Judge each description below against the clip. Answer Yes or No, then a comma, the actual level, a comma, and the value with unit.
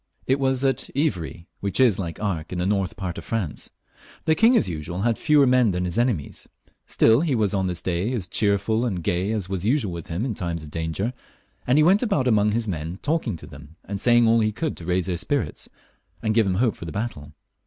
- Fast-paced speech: Yes, fast, 240 wpm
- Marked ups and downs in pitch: Yes, wide, 5.8 semitones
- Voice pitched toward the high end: No, low, 100 Hz